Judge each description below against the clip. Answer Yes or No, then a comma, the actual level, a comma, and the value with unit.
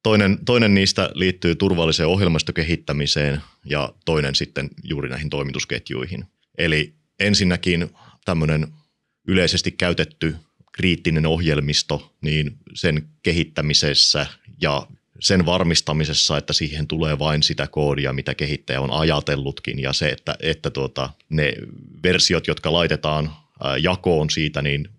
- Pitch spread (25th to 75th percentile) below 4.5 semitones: Yes, average, 2.7 semitones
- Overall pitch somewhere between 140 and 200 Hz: No, very low, 75 Hz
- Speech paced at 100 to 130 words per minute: Yes, average, 115 wpm